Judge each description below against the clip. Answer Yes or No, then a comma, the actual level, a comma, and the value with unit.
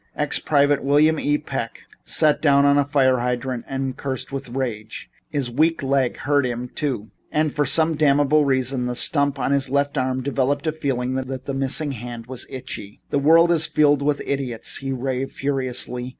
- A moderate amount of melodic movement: No, narrow, 2.1 semitones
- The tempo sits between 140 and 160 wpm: No, average, 185 wpm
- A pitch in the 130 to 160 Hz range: Yes, low, 135 Hz